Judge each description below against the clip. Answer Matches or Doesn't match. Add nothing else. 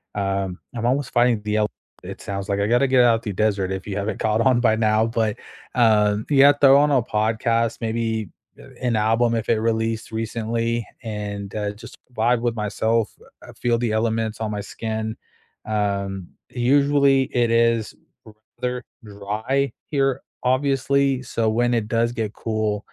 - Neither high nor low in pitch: Doesn't match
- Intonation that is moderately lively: Doesn't match